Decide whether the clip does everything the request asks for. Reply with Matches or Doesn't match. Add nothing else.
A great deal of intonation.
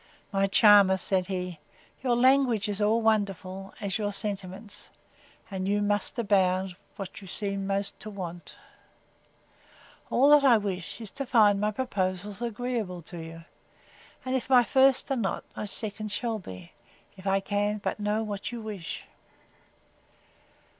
Doesn't match